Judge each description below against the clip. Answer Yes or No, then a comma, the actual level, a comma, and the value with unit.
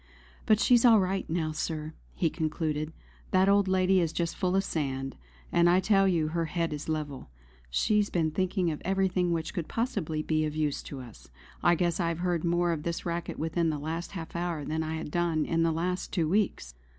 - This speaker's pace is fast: Yes, fast, 210 wpm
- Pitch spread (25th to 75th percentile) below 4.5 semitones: Yes, average, 2.7 semitones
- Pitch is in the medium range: Yes, medium, 170 Hz